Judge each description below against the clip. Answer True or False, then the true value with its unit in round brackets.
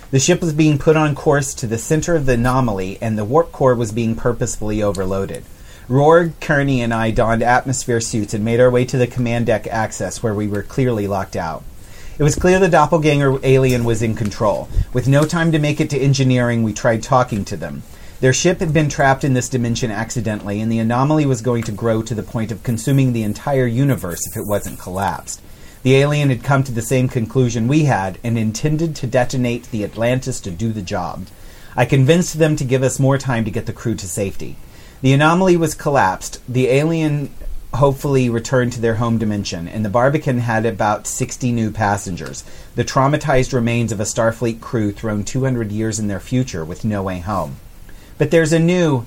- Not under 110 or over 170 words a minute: False (205 wpm)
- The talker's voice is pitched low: True (120 Hz)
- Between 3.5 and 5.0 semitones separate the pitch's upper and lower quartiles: True (4.0 semitones)